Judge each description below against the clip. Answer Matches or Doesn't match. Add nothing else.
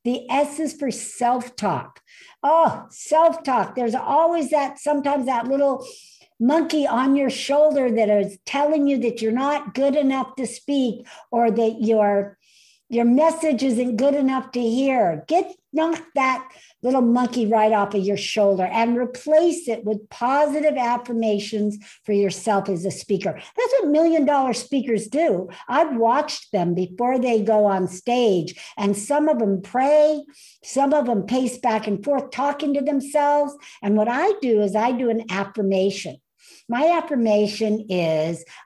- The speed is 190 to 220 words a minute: Doesn't match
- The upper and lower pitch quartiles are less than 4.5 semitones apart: Doesn't match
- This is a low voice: Doesn't match